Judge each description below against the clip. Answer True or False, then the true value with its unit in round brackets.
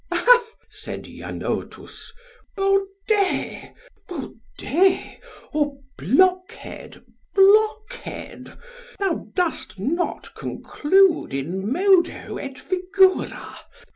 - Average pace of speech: False (70 wpm)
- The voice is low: False (370 Hz)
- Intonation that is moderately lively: True (5.0 semitones)